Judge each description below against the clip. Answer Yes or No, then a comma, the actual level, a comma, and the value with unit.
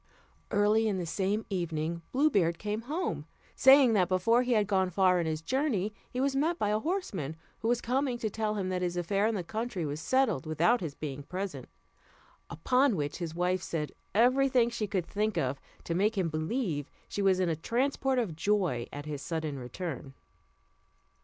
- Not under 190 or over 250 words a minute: Yes, average, 195 wpm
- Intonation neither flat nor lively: No, wide, 6.1 semitones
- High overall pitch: Yes, high, 195 Hz